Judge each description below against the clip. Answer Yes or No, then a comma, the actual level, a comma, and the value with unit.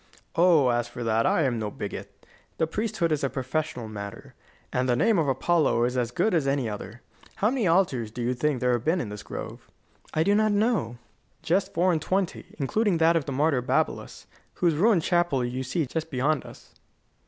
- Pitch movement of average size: No, wide, 5.8 semitones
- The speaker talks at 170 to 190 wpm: No, fast, 205 wpm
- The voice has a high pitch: No, medium, 150 Hz